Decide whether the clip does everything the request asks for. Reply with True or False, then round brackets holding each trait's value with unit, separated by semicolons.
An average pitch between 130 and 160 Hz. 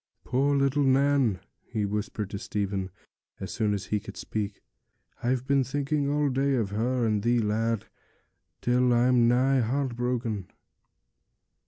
False (120 Hz)